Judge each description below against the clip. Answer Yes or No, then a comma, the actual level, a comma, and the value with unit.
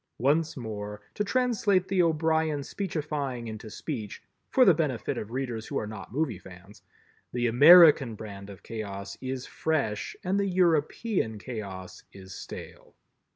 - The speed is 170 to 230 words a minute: No, slow, 135 wpm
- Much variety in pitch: Yes, wide, 7.1 semitones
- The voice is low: Yes, low, 130 Hz